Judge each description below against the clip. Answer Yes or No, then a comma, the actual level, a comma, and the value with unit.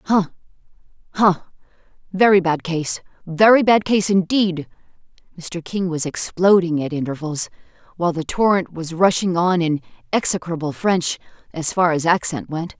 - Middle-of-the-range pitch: Yes, medium, 175 Hz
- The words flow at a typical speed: No, slow, 125 wpm